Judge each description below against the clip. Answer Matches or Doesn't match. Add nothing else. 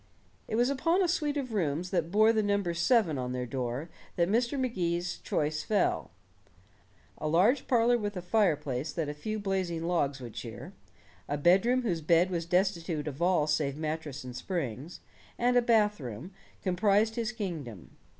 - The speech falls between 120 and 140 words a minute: Doesn't match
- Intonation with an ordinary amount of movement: Doesn't match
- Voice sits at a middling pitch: Matches